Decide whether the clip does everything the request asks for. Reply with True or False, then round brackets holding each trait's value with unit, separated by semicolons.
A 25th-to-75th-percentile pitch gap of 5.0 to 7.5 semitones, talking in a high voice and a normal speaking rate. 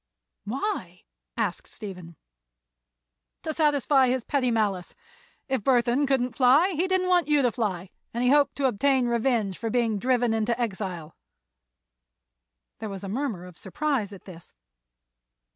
True (5.3 semitones; 240 Hz; 145 wpm)